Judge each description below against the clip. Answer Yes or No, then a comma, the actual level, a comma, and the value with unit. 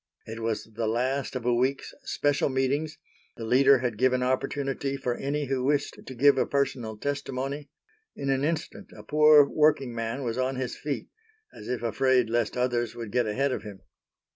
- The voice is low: Yes, low, 130 Hz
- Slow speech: No, average, 185 wpm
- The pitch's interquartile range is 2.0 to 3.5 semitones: Yes, average, 2.7 semitones